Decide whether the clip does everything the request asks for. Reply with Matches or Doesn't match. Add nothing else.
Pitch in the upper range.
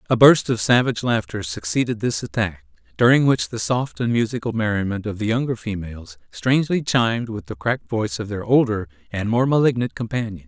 Doesn't match